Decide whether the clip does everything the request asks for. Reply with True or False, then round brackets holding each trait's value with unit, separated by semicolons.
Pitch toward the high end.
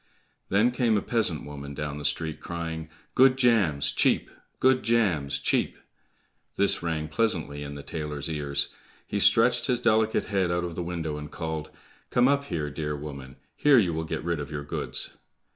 False (80 Hz)